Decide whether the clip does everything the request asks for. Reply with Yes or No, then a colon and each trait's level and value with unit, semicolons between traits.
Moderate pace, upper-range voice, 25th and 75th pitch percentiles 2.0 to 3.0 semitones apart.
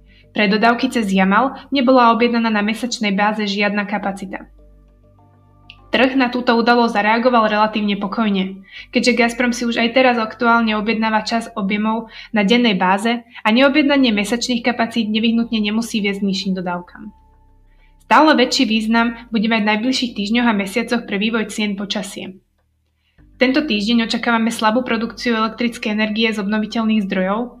Yes: average, 140 wpm; high, 225 Hz; narrow, 2.5 semitones